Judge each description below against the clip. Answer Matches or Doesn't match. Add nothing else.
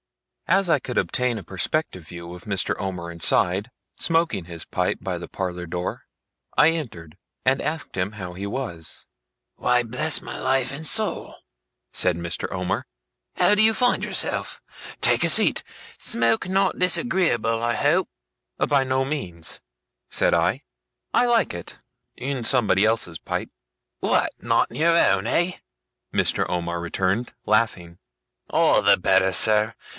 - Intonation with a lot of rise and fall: Matches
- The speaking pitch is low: Matches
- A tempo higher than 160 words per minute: Doesn't match